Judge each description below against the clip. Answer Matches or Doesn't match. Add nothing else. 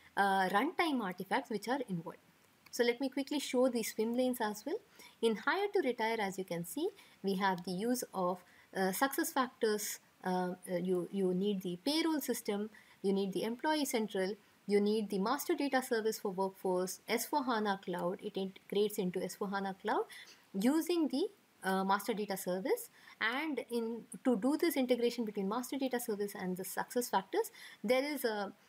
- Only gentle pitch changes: Doesn't match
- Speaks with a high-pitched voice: Matches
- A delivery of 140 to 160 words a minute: Doesn't match